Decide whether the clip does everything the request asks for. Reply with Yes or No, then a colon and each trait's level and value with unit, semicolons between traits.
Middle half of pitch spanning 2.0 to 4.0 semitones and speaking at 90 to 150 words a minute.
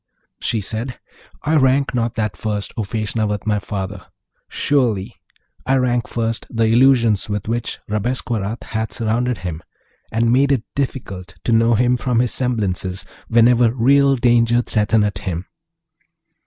Yes: average, 3.0 semitones; average, 140 wpm